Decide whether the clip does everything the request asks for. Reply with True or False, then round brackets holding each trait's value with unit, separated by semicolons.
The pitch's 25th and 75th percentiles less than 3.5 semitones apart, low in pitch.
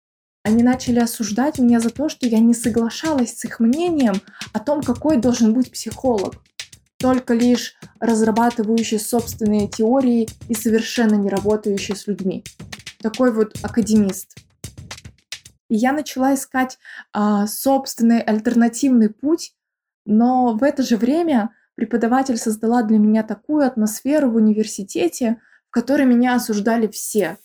False (2.7 semitones; 235 Hz)